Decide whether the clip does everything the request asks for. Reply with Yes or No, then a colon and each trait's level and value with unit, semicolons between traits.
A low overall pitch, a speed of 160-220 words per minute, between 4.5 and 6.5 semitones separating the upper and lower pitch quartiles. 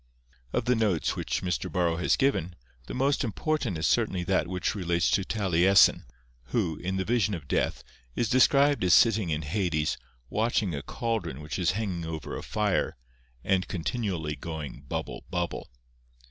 Yes: very low, 95 Hz; average, 165 wpm; average, 5.0 semitones